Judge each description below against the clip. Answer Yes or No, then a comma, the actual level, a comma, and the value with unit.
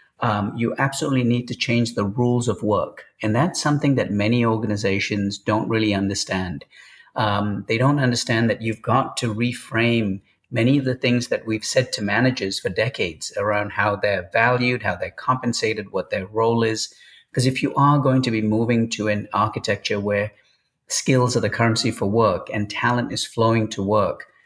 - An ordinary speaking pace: No, fast, 180 wpm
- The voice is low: Yes, low, 115 Hz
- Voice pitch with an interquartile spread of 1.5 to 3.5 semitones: Yes, average, 2.9 semitones